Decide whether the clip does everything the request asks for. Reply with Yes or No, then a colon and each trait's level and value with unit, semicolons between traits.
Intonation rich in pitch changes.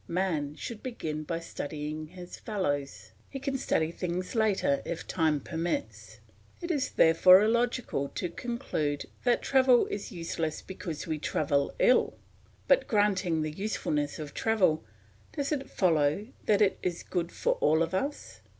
Yes: wide, 6.2 semitones